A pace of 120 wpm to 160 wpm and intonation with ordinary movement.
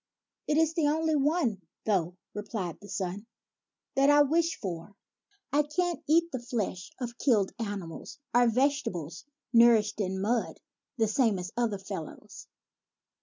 No: average, 150 wpm; wide, 6.9 semitones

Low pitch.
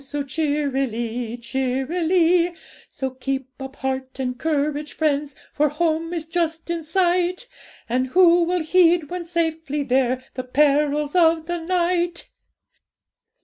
No: very high, 300 Hz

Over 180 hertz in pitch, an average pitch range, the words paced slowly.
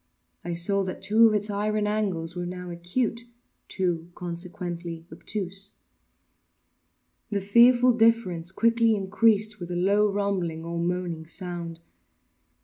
Yes: high, 190 Hz; average, 3.6 semitones; slow, 120 wpm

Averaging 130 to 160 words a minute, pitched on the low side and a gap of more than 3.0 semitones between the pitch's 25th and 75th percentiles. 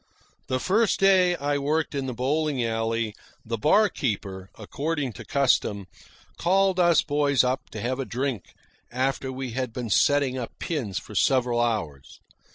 Yes: average, 155 wpm; low, 130 Hz; average, 4.4 semitones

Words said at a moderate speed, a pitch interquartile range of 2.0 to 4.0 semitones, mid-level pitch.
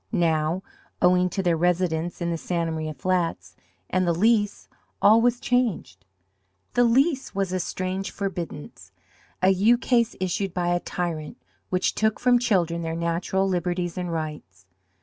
Yes: average, 150 wpm; average, 3.0 semitones; medium, 180 Hz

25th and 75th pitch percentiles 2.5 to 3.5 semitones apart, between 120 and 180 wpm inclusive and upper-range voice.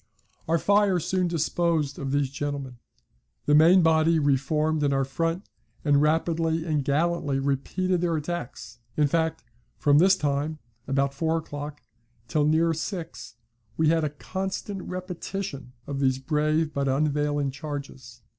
No: average, 2.9 semitones; average, 145 wpm; medium, 155 Hz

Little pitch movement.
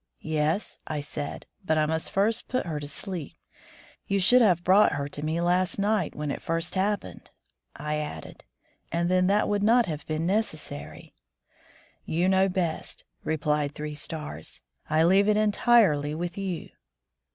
No: average, 4.5 semitones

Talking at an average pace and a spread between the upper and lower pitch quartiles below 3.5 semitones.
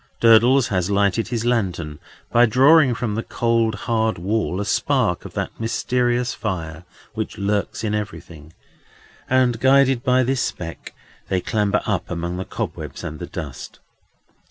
No: average, 150 wpm; average, 4.3 semitones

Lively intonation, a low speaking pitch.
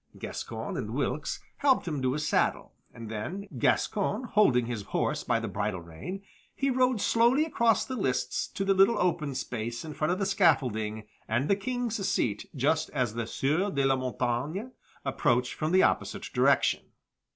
No: wide, 8.7 semitones; medium, 155 Hz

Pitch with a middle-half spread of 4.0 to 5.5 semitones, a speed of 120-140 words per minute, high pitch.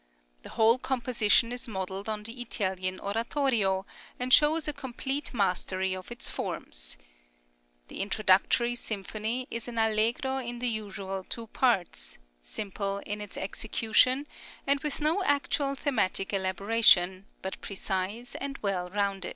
Yes: average, 4.6 semitones; slow, 135 wpm; high, 220 Hz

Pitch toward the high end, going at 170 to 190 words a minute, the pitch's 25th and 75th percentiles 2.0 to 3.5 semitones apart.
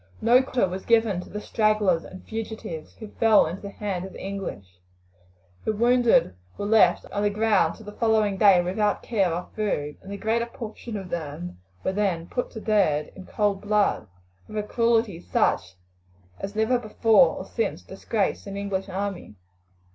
Yes: high, 205 Hz; average, 180 wpm; average, 2.9 semitones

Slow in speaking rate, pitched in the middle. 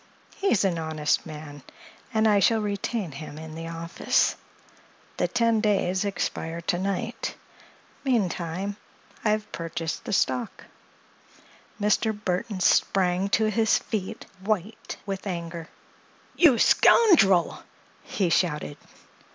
No: slow, 110 wpm; high, 195 Hz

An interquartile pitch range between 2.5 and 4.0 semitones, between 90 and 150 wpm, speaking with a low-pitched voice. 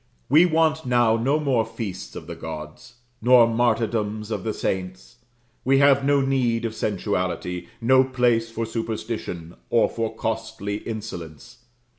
Yes: average, 3.5 semitones; average, 140 wpm; low, 115 Hz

